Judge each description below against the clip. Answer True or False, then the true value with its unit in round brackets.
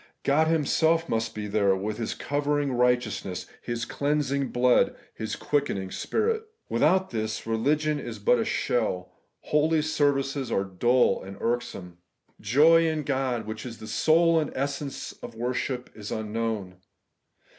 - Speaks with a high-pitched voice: False (125 Hz)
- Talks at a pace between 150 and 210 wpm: False (140 wpm)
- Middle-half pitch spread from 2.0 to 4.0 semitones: False (5.1 semitones)